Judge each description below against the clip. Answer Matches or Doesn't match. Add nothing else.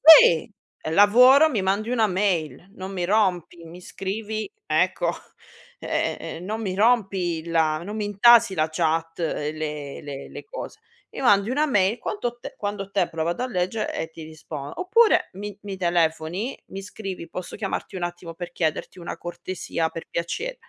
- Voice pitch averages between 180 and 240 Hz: Matches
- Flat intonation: Doesn't match